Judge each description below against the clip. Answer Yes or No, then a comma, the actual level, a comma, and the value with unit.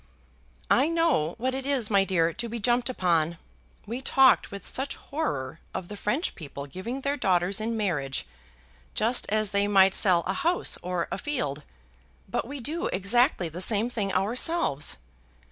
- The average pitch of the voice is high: Yes, high, 210 Hz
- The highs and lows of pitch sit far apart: Yes, wide, 6.2 semitones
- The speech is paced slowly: No, average, 165 wpm